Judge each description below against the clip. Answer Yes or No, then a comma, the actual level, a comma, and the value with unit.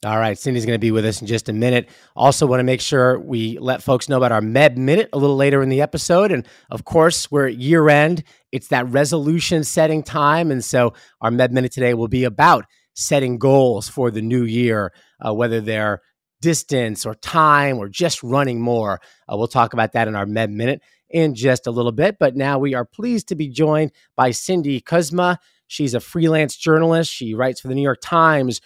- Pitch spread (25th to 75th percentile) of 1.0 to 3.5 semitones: No, average, 4.5 semitones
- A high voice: No, low, 130 Hz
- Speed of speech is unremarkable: No, fast, 220 wpm